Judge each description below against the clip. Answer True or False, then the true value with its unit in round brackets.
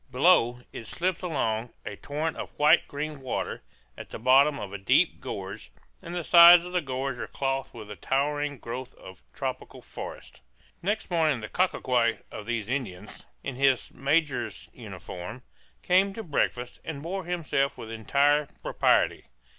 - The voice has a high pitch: False (140 Hz)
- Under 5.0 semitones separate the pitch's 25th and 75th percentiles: False (5.3 semitones)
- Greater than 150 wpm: True (160 wpm)